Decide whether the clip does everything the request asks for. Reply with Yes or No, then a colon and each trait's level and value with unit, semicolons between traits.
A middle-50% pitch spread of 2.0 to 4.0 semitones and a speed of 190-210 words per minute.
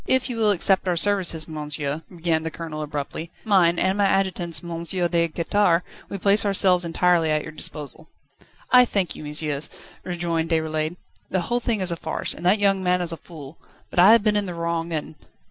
Yes: average, 3.2 semitones; average, 200 wpm